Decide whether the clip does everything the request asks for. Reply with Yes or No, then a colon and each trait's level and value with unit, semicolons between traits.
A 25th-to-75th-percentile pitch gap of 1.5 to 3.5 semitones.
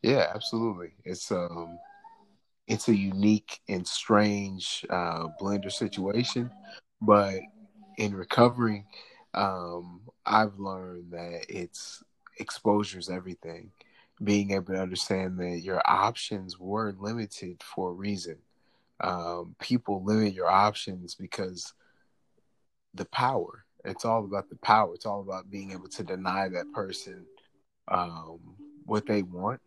Yes: average, 2.8 semitones